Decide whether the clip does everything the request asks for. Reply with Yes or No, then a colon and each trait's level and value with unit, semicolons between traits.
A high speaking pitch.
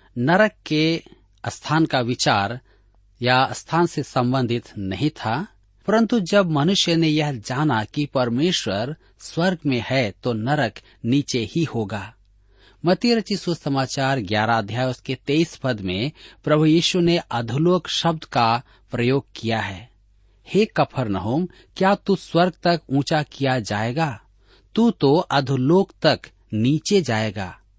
No: low, 135 Hz